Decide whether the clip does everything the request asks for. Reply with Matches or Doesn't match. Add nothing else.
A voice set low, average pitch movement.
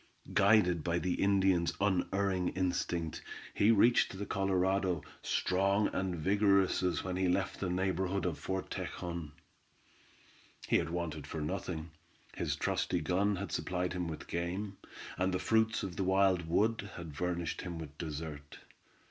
Doesn't match